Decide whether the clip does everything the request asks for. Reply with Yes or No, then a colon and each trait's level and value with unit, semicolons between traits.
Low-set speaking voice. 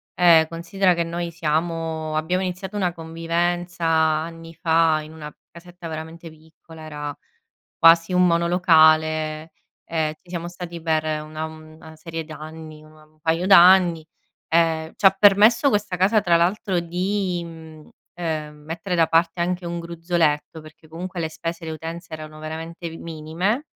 No: medium, 165 Hz